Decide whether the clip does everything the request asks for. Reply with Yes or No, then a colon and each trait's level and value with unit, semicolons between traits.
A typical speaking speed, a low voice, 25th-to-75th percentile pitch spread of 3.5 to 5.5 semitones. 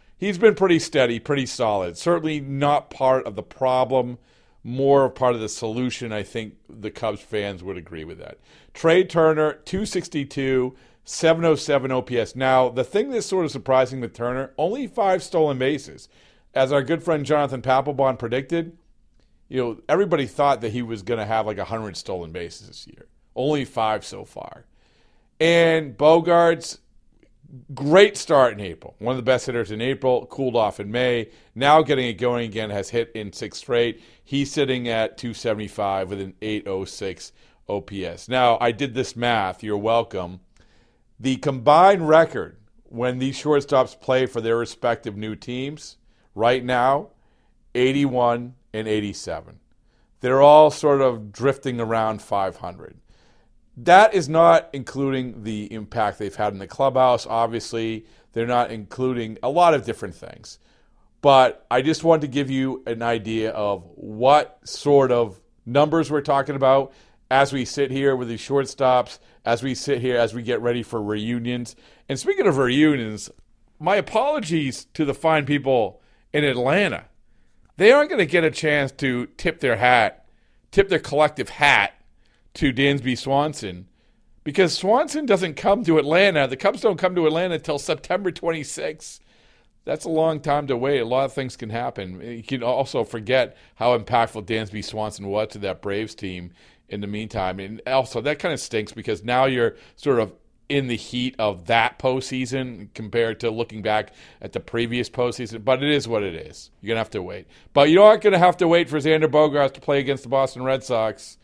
Yes: average, 170 wpm; low, 130 Hz; average, 4.4 semitones